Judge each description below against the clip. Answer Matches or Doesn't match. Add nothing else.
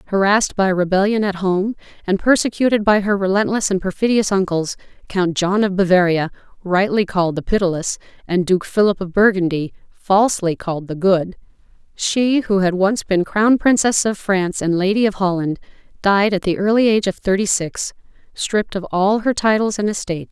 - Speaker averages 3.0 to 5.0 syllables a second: Doesn't match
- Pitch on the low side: Doesn't match